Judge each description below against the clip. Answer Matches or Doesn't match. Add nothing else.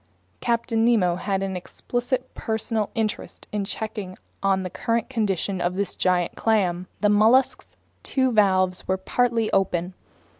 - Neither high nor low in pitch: Doesn't match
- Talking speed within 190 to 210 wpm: Doesn't match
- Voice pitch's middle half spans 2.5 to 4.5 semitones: Matches